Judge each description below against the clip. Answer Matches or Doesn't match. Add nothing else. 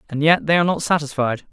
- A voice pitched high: Doesn't match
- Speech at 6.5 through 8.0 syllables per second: Matches